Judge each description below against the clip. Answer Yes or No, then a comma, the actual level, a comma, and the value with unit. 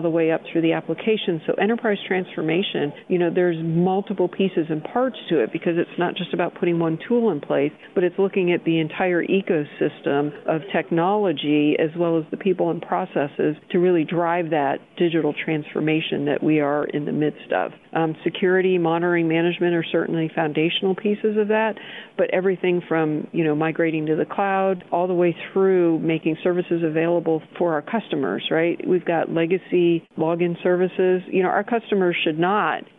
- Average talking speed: Yes, average, 180 wpm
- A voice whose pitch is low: No, medium, 175 Hz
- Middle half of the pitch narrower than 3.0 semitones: Yes, narrow, 2.4 semitones